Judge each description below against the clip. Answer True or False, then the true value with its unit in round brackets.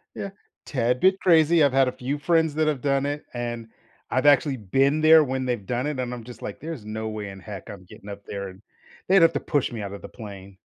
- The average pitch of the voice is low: True (130 Hz)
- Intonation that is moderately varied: False (5.7 semitones)